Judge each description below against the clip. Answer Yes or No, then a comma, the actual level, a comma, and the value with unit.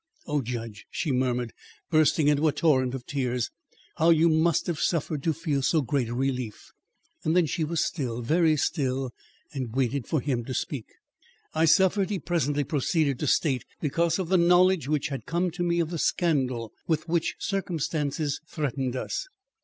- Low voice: No, medium, 150 Hz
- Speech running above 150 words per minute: Yes, average, 175 wpm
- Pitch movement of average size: Yes, average, 4.3 semitones